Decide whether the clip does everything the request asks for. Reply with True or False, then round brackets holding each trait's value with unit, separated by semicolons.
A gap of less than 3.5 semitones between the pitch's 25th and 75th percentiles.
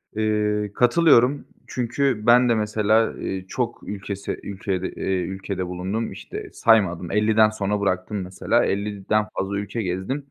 True (2.8 semitones)